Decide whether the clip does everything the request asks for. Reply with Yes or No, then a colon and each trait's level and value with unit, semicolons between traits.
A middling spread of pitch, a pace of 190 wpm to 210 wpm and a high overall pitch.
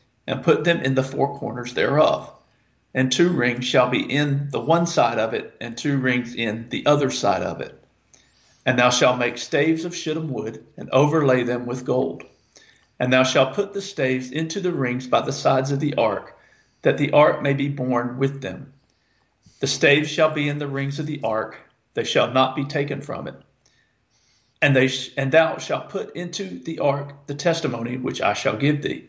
No: average, 3.2 semitones; average, 200 wpm; medium, 140 Hz